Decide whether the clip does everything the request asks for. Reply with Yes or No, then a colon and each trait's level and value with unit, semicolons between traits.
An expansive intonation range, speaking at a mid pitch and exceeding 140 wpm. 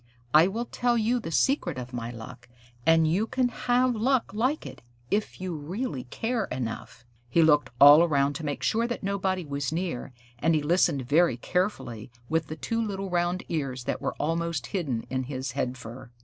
Yes: wide, 6.9 semitones; medium, 165 Hz; average, 190 wpm